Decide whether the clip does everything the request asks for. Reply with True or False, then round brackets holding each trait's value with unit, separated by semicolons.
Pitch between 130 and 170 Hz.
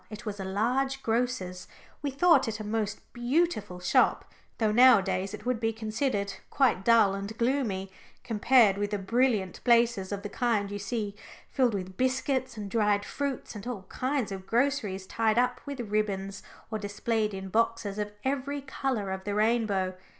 False (220 Hz)